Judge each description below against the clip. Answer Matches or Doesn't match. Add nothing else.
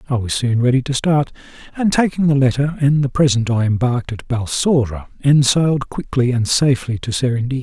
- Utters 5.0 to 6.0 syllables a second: Matches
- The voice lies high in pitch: Doesn't match